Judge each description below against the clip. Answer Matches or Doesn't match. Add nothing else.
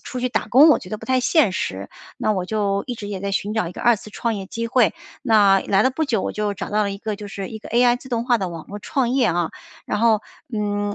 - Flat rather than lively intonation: Doesn't match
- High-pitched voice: Matches